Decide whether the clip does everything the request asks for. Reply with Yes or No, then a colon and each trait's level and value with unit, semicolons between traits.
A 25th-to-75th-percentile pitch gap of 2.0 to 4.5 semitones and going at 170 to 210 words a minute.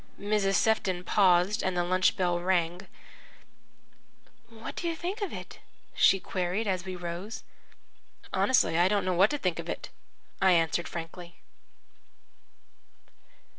No: average, 2.9 semitones; slow, 135 wpm